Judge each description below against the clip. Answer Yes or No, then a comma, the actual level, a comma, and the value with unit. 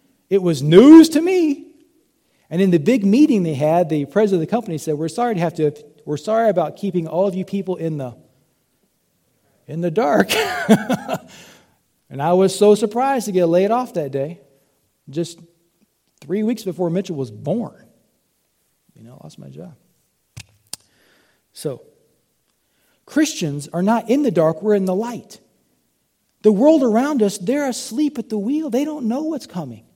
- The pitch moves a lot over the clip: Yes, wide, 6.5 semitones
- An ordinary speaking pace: Yes, average, 170 wpm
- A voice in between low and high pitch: No, high, 195 Hz